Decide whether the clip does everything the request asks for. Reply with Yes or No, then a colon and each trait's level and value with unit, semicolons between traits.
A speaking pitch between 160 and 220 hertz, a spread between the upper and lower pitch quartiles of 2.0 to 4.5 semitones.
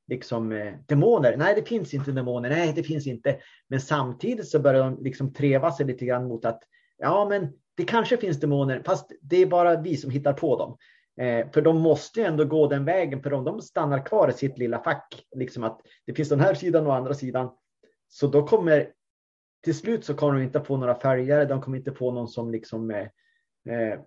No: medium, 140 Hz; average, 3.7 semitones